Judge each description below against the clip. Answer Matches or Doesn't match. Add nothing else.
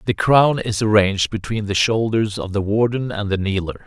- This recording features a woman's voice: Doesn't match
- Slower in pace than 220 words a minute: Matches